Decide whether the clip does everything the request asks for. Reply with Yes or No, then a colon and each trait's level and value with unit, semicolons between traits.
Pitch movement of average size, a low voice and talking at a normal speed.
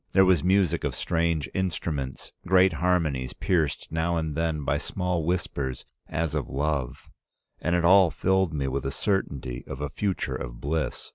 Yes: average, 4.3 semitones; very low, 80 Hz; average, 165 wpm